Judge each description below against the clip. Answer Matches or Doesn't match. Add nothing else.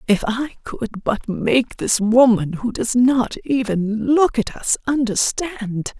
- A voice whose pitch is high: Matches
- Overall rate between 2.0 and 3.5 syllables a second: Matches